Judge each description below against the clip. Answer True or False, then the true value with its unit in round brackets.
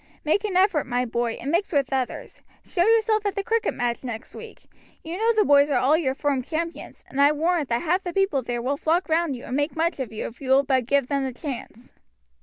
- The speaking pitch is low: False (285 Hz)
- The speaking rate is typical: False (245 wpm)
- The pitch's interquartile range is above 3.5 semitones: True (5.1 semitones)